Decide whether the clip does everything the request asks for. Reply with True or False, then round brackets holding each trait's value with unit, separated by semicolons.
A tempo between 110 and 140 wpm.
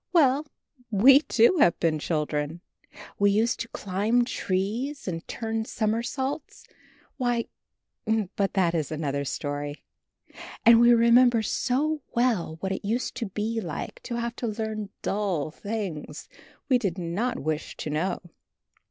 True (135 wpm)